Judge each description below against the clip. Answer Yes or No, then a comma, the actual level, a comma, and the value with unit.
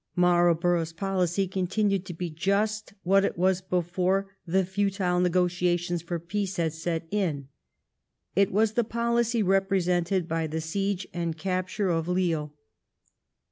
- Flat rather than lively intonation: Yes, narrow, 2.3 semitones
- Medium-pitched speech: Yes, medium, 180 Hz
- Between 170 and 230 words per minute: No, slow, 135 wpm